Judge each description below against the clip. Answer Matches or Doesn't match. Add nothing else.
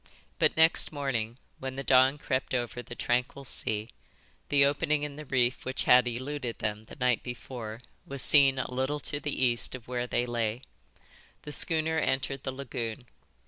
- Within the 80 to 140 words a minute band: Doesn't match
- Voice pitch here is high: Doesn't match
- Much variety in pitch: Doesn't match